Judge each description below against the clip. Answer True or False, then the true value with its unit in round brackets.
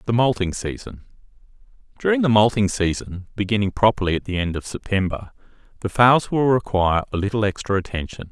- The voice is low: True (105 Hz)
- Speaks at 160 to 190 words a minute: False (150 wpm)